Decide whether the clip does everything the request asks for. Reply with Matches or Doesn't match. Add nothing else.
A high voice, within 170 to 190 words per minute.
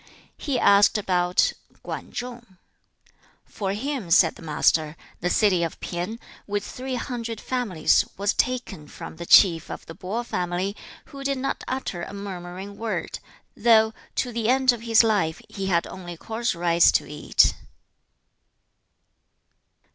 Doesn't match